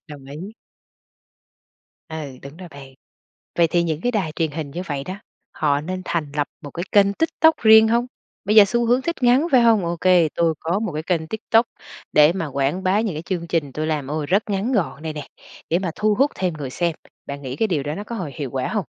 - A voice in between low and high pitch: Yes, medium, 170 Hz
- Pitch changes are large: Yes, wide, 5.7 semitones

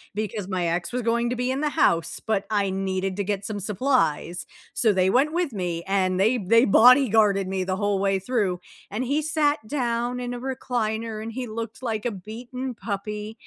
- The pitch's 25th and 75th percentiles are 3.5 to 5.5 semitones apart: Yes, average, 4.2 semitones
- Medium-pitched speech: No, high, 215 Hz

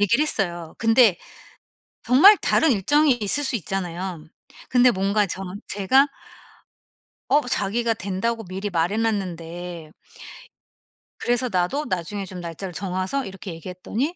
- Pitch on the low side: No, high, 195 Hz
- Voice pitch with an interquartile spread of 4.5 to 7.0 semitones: Yes, average, 5.0 semitones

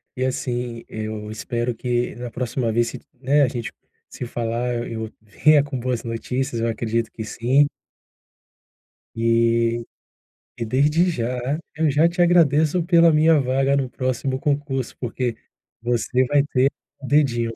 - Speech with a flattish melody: No, average, 3.5 semitones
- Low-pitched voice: Yes, low, 125 Hz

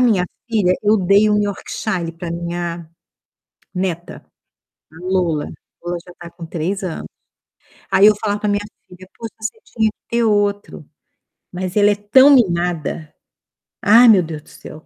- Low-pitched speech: No, high, 190 Hz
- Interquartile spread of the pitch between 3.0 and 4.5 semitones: Yes, average, 3.4 semitones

